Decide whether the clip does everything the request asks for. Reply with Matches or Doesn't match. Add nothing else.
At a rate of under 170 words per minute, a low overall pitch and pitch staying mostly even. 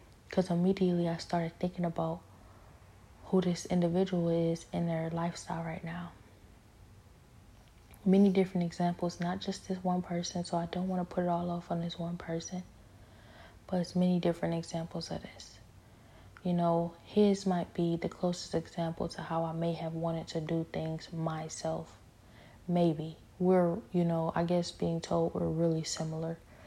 Doesn't match